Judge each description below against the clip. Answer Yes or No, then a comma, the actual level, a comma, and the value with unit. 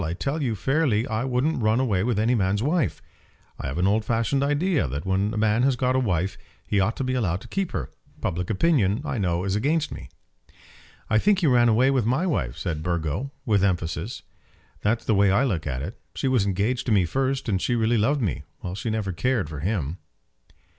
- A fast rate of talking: Yes, fast, 220 wpm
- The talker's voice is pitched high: No, low, 110 Hz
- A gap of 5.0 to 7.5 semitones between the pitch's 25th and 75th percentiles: Yes, wide, 5.6 semitones